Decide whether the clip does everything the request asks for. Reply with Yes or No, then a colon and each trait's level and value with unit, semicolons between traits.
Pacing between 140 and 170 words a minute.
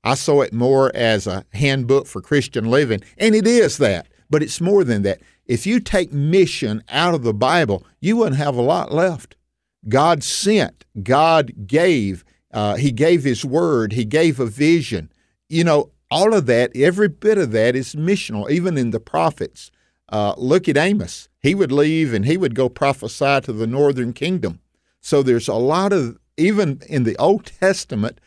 No: average, 185 wpm